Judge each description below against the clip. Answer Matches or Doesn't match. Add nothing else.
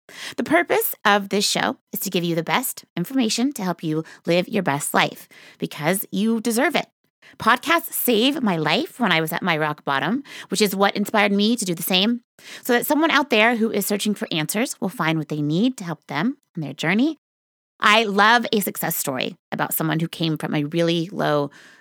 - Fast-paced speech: Matches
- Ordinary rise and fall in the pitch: Doesn't match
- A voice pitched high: Matches